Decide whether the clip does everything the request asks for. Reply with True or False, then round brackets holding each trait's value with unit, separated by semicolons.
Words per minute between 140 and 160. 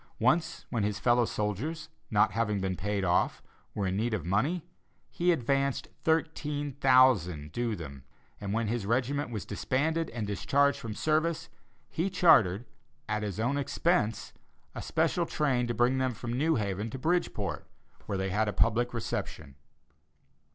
True (155 wpm)